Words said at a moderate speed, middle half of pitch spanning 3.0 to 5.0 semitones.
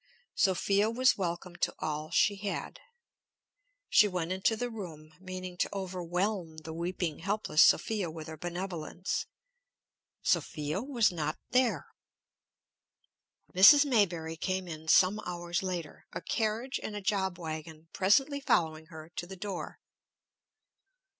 No: slow, 125 wpm; average, 3.9 semitones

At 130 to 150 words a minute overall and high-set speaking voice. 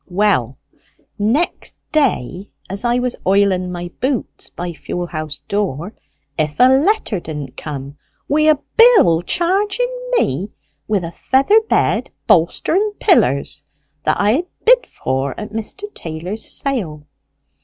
Yes: slow, 135 wpm; high, 205 Hz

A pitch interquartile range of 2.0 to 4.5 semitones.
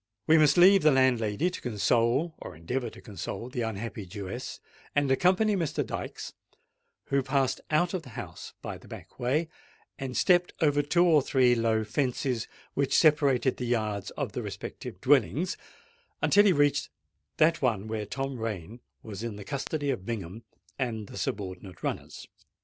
No: average, 5.3 semitones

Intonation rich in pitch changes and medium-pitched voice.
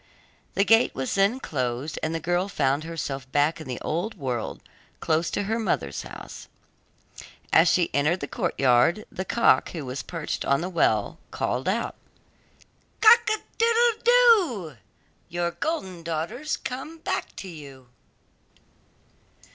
Yes: wide, 8.1 semitones; medium, 170 Hz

